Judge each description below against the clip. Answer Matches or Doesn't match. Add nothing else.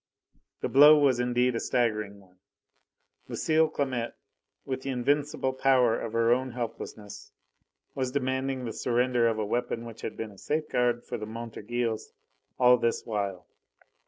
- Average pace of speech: Matches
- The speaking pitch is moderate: Doesn't match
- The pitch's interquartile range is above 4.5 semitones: Doesn't match